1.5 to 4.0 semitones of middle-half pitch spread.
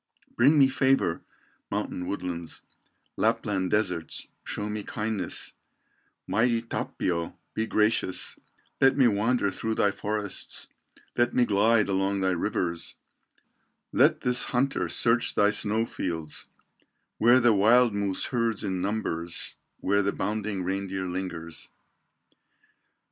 Yes: average, 3.6 semitones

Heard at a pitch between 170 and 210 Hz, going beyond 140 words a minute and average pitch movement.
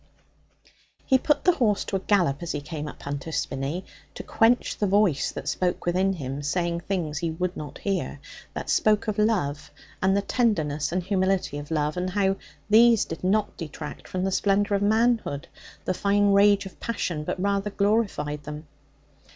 Yes: high, 190 Hz; average, 185 wpm; average, 4.9 semitones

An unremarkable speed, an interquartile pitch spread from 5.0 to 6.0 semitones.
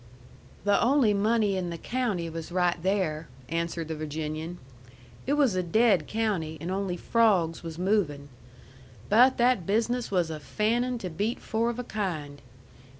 Yes: average, 155 wpm; average, 5.3 semitones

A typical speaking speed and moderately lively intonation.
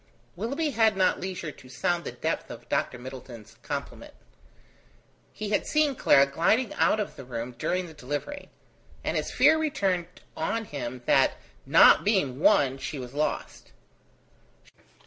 No: average, 145 wpm; wide, 8.5 semitones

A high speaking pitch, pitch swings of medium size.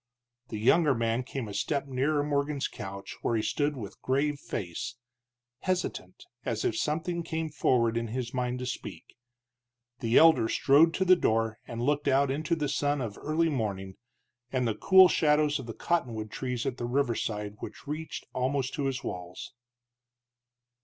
No: low, 135 Hz; average, 4.5 semitones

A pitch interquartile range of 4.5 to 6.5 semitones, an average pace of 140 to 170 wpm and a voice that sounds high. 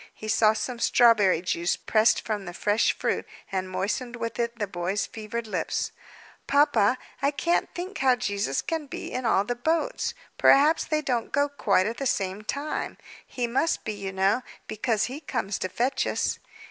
No: average, 4.9 semitones; average, 180 wpm; high, 230 Hz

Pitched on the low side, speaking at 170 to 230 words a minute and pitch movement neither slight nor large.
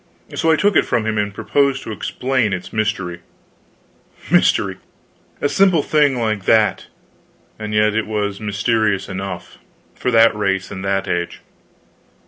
No: low, 105 Hz; average, 150 wpm; average, 3.4 semitones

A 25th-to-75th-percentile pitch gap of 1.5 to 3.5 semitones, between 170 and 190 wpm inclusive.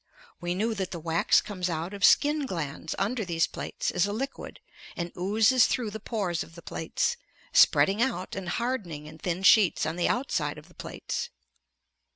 No: average, 4.6 semitones; average, 185 wpm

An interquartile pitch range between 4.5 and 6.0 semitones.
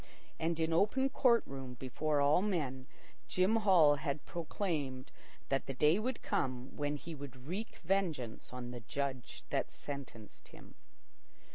Yes: wide, 5.6 semitones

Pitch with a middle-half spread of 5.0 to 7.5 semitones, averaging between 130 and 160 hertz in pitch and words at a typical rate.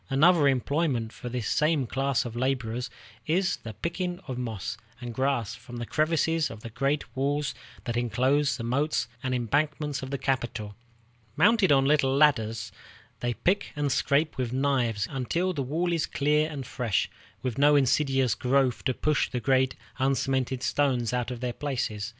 No: average, 3.3 semitones; low, 135 Hz; average, 170 wpm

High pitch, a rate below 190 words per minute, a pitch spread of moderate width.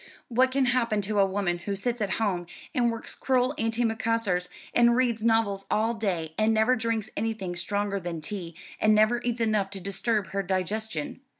Yes: high, 215 Hz; average, 180 wpm; average, 3.0 semitones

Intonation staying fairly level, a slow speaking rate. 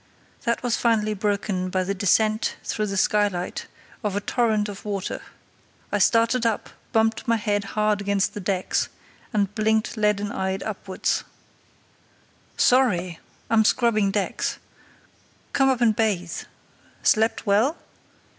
Yes: narrow, 2.0 semitones; slow, 130 wpm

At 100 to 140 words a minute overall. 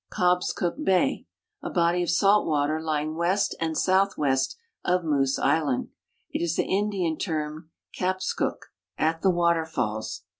Yes: slow, 135 wpm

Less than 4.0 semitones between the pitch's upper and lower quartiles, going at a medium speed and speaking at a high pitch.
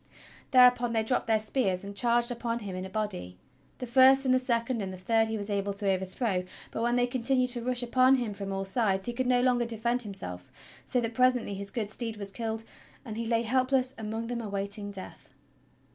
No: average, 3.6 semitones; fast, 220 wpm; high, 230 Hz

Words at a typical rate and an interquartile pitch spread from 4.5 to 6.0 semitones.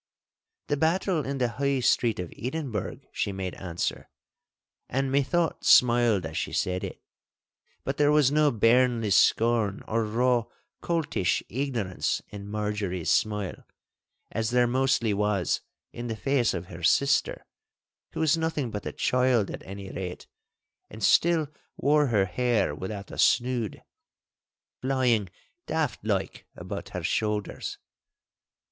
No: slow, 130 wpm; average, 5.1 semitones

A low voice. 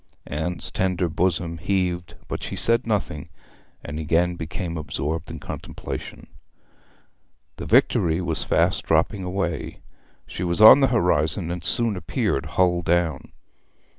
Yes: very low, 85 Hz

